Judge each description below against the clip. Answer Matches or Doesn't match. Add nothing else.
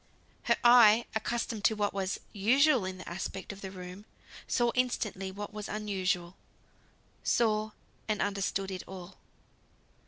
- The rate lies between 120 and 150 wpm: Matches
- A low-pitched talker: Doesn't match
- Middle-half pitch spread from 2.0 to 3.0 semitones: Matches